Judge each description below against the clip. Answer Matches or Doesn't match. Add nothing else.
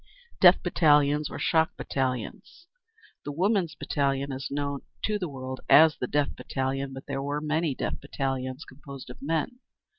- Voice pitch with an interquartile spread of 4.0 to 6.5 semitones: Doesn't match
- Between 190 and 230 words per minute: Doesn't match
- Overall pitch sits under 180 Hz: Matches